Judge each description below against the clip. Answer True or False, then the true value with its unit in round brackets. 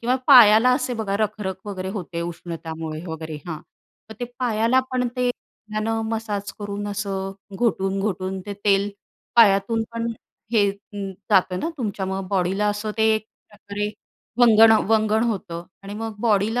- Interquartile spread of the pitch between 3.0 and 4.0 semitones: False (2.5 semitones)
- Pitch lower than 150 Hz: False (205 Hz)